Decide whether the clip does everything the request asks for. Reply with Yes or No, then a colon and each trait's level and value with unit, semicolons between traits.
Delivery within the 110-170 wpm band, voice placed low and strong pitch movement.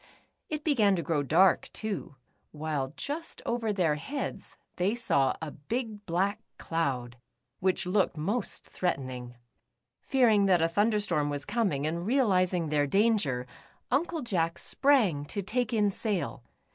No: average, 140 wpm; medium, 185 Hz; wide, 6.6 semitones